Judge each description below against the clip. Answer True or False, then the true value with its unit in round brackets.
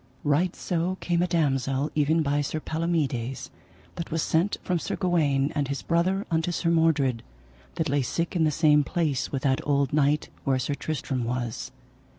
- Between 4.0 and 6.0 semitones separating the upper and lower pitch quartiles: False (3.4 semitones)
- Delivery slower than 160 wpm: False (175 wpm)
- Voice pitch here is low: False (150 Hz)